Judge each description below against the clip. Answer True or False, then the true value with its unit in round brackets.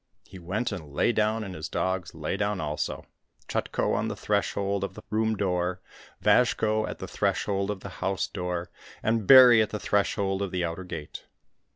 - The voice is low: True (95 Hz)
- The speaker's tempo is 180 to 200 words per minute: True (185 wpm)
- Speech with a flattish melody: False (3.0 semitones)